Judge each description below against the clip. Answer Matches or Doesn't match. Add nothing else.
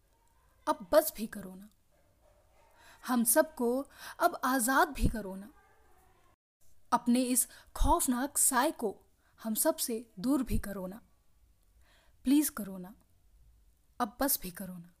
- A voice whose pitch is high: Matches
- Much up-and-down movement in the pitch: Matches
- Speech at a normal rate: Matches